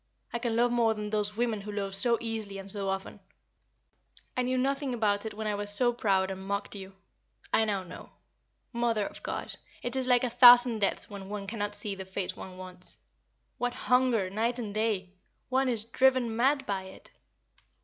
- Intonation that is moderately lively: Yes, average, 3.4 semitones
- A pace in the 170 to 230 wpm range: Yes, average, 195 wpm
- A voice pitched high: Yes, high, 215 Hz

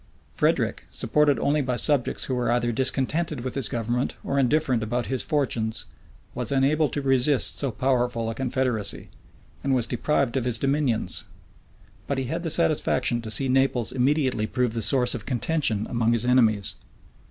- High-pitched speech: No, low, 125 Hz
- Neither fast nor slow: Yes, average, 165 wpm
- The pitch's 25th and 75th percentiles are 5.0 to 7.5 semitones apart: No, average, 2.8 semitones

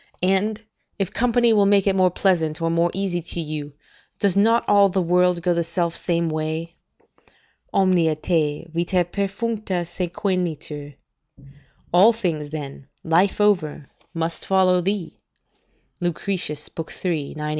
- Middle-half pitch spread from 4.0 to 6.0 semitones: No, average, 3.2 semitones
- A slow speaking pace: Yes, slow, 130 wpm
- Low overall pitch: No, medium, 175 Hz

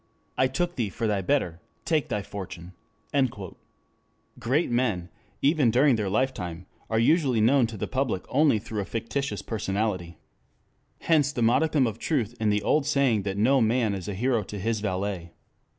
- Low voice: Yes, low, 115 Hz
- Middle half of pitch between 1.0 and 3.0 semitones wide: No, average, 4.9 semitones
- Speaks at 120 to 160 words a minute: No, average, 170 wpm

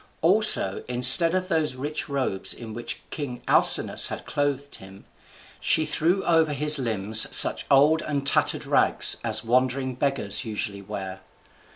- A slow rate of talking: No, average, 145 wpm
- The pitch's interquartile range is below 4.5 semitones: No, average, 4.8 semitones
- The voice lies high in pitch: No, low, 135 Hz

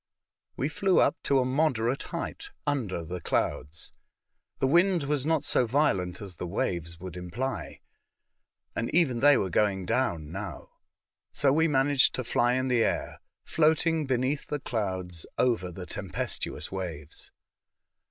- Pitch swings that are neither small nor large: No, wide, 8.0 semitones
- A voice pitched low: Yes, low, 125 Hz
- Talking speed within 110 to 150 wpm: Yes, average, 145 wpm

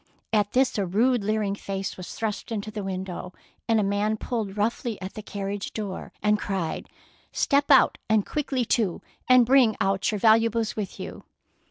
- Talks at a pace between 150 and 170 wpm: No, average, 185 wpm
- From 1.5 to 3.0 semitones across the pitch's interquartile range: Yes, narrow, 2.5 semitones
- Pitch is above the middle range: Yes, high, 210 Hz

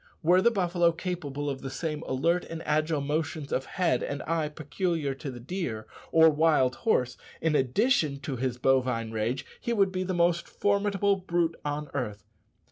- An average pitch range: Yes, average, 4.7 semitones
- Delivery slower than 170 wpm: No, average, 175 wpm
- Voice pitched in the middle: Yes, medium, 155 Hz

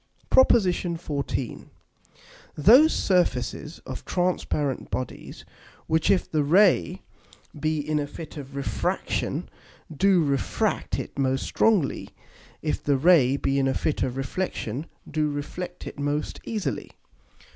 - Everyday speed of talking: No, slow, 125 wpm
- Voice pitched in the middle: Yes, medium, 150 Hz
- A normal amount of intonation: Yes, average, 4.5 semitones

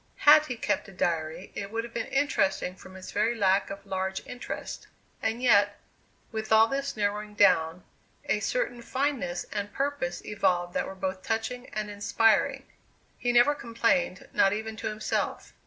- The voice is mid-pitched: No, high, 215 Hz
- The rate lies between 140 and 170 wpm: Yes, average, 165 wpm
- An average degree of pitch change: Yes, average, 3.9 semitones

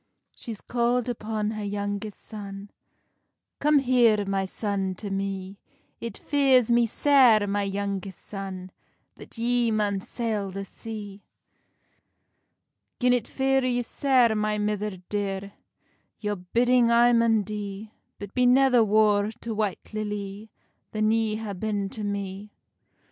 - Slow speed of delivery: Yes, slow, 130 wpm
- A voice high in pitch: Yes, high, 210 Hz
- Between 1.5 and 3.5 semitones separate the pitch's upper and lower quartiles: Yes, average, 2.8 semitones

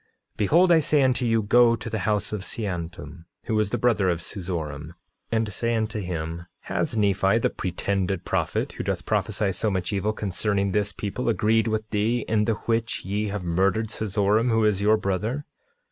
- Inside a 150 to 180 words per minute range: No, average, 190 wpm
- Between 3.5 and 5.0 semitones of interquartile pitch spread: No, average, 2.7 semitones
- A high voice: No, low, 105 Hz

